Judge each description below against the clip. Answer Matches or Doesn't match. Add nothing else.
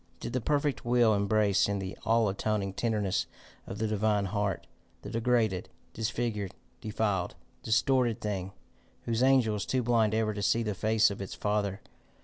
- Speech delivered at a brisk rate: Doesn't match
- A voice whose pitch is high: Doesn't match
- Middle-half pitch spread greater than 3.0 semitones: Doesn't match